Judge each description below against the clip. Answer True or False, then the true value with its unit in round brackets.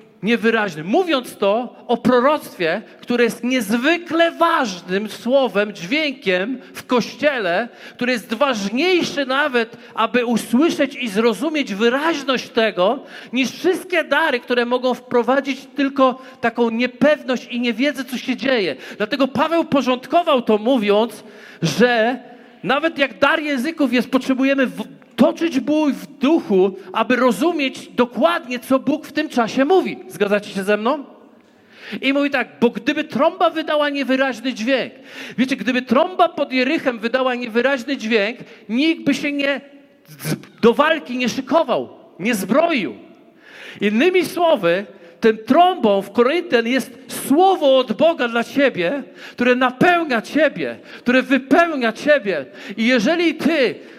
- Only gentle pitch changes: False (3.7 semitones)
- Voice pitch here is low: False (255 Hz)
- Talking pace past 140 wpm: False (125 wpm)